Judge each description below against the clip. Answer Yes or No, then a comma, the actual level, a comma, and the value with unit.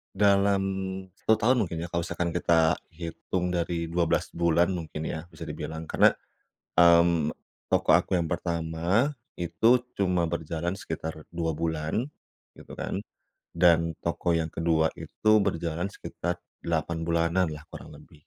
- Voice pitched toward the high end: No, very low, 85 Hz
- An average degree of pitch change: No, narrow, 1.6 semitones